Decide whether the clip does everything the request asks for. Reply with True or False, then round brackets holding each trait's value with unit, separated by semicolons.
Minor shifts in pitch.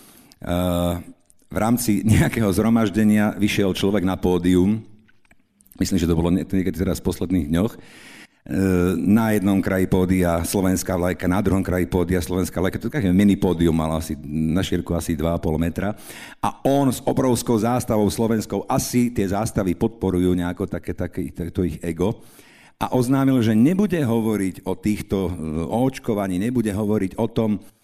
False (3.5 semitones)